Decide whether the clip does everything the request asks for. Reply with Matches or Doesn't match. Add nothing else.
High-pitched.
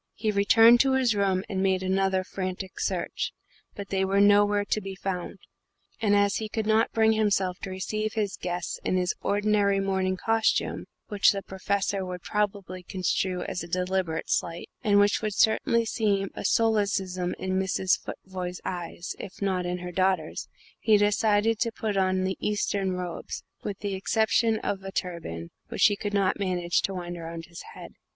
Matches